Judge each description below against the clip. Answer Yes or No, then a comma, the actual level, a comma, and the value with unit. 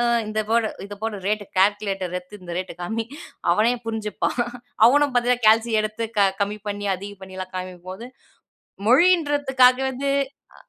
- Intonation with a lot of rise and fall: No, average, 3.5 semitones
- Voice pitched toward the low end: No, high, 215 Hz